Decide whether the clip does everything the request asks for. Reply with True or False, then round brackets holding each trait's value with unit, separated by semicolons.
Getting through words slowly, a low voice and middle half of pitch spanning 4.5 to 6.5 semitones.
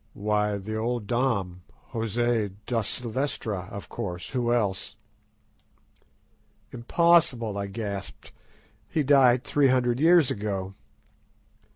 False (95 wpm; 115 Hz; 3.9 semitones)